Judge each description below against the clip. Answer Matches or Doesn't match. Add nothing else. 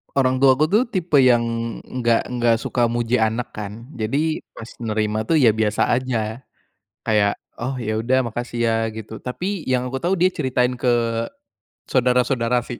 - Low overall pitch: Matches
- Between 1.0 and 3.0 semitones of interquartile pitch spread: Matches